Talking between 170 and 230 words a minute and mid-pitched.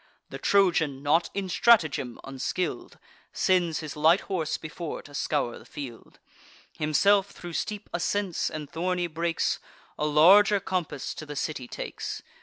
No: average, 140 wpm; medium, 165 Hz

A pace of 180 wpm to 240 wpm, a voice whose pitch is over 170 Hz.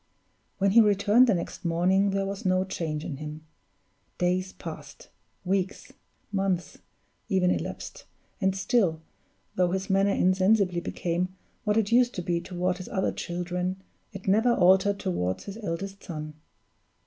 No: average, 145 wpm; high, 190 Hz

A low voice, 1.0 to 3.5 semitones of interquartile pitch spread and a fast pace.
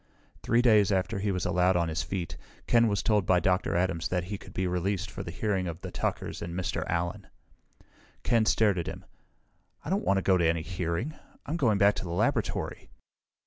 Yes: very low, 95 Hz; average, 2.9 semitones; fast, 210 wpm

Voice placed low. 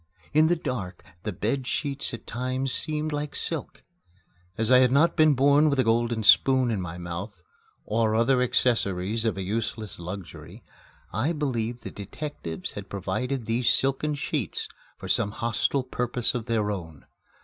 Yes: low, 120 Hz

